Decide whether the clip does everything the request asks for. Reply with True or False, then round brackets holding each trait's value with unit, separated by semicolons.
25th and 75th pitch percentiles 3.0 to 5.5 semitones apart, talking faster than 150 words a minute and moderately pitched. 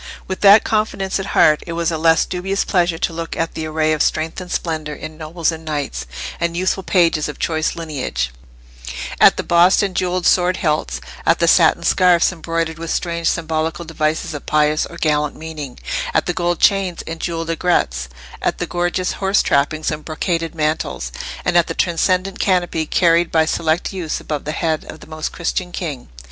False (2.4 semitones; 185 wpm; 165 Hz)